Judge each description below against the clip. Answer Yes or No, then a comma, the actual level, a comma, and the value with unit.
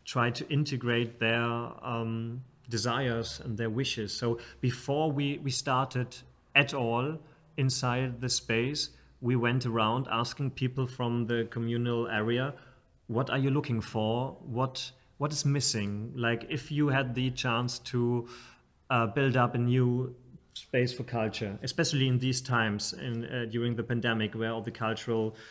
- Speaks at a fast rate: No, average, 155 wpm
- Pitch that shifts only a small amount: Yes, narrow, 2.2 semitones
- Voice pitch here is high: No, low, 120 Hz